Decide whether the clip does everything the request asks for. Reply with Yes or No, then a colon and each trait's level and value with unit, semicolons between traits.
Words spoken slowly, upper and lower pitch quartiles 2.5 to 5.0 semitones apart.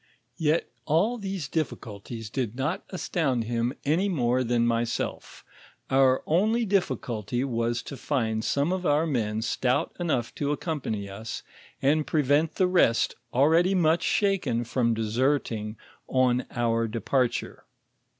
No: slow, 130 wpm; wide, 5.5 semitones